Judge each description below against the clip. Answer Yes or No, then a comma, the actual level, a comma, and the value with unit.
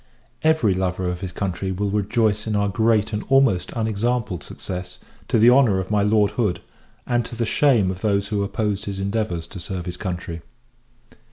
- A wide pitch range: No, average, 3.1 semitones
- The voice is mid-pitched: No, low, 100 Hz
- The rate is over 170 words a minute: Yes, average, 185 wpm